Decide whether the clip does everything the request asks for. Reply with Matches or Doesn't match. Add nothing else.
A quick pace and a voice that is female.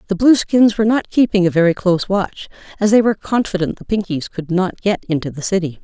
Matches